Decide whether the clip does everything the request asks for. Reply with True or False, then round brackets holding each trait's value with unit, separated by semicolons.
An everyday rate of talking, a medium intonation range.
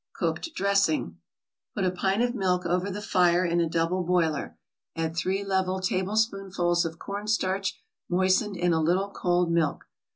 False (155 wpm; 2.3 semitones)